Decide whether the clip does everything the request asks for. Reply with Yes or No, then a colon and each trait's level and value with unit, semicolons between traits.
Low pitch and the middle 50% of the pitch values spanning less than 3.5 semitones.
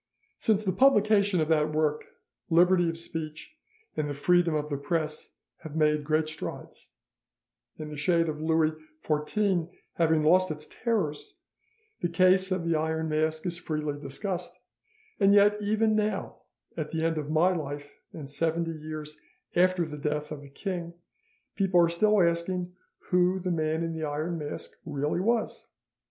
No: medium, 165 Hz; average, 3.1 semitones